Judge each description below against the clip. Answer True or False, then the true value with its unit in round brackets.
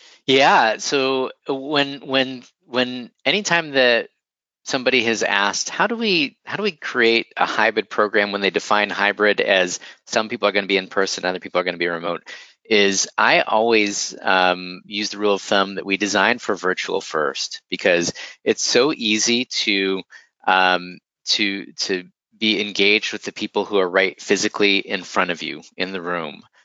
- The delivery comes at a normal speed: True (180 wpm)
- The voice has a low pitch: True (105 Hz)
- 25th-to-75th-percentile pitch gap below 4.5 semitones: False (5.1 semitones)